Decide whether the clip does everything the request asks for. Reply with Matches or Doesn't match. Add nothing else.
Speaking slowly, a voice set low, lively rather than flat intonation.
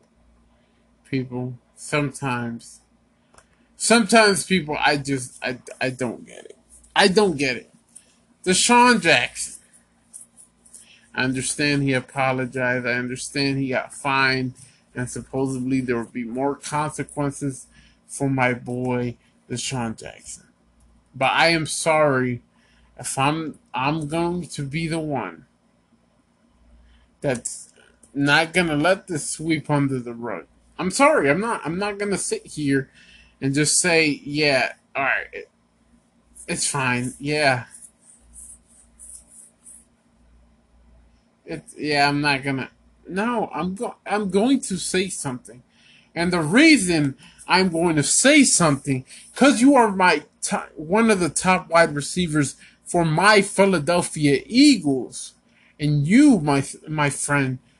Doesn't match